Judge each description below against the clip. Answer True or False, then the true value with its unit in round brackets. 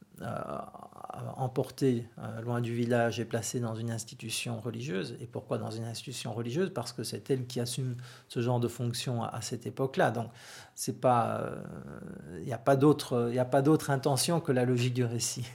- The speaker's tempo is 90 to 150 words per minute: False (180 wpm)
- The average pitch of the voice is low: True (125 Hz)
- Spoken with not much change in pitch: True (2.2 semitones)